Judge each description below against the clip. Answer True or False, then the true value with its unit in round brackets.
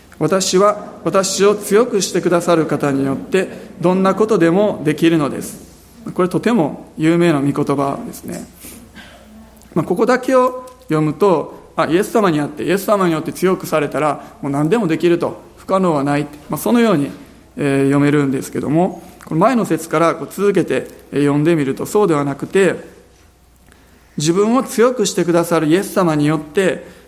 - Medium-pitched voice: True (170 Hz)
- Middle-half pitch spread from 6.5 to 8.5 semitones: False (5.5 semitones)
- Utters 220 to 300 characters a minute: False (340 characters per minute)